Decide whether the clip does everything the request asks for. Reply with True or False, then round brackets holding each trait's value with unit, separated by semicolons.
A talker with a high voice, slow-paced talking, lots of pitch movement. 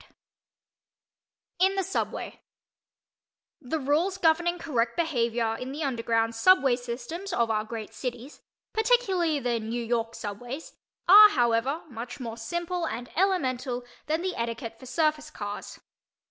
True (255 Hz; 130 wpm; 6.6 semitones)